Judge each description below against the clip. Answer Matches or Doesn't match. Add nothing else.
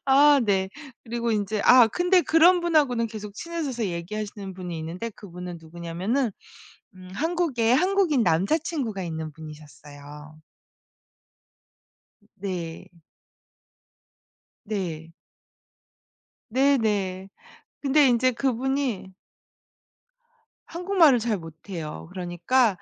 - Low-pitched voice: Doesn't match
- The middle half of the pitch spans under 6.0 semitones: Doesn't match